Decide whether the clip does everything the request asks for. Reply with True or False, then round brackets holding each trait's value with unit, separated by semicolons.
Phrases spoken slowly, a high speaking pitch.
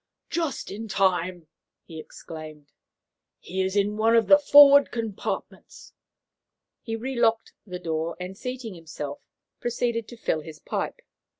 True (130 wpm; 200 Hz)